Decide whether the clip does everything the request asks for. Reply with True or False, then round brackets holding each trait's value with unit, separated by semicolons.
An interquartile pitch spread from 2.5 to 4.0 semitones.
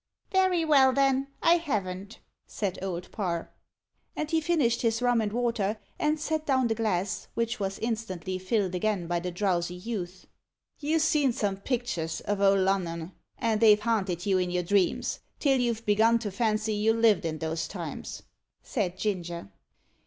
False (4.6 semitones)